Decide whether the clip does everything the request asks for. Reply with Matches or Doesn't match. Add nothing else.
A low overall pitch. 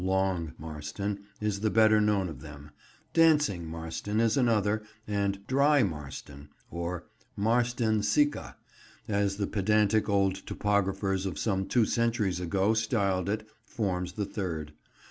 Matches